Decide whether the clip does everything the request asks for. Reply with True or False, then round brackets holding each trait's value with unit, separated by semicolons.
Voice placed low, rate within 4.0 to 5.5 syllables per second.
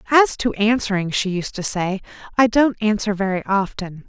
False (210 Hz; 5.0 syllables/s)